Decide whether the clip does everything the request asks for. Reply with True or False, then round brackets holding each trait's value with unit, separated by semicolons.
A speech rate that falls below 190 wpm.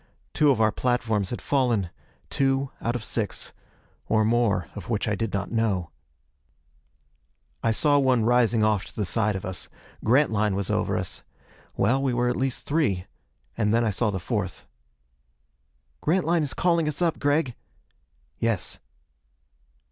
True (155 wpm)